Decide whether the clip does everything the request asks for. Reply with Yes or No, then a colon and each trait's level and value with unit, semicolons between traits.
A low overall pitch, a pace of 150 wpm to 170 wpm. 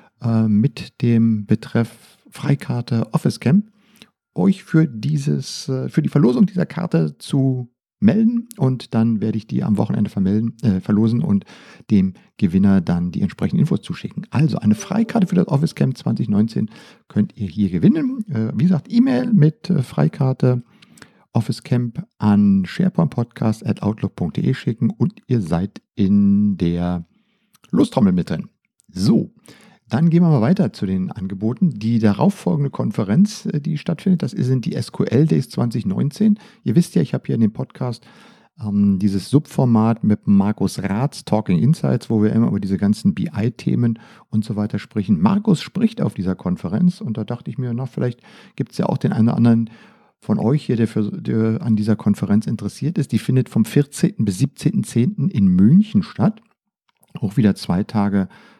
Yes: low, 125 Hz; average, 165 wpm